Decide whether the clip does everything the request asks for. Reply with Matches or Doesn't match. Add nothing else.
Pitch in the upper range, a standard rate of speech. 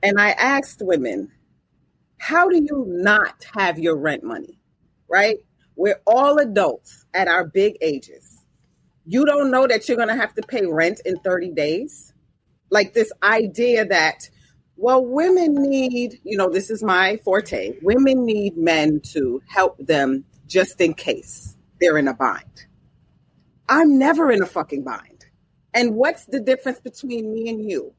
Matches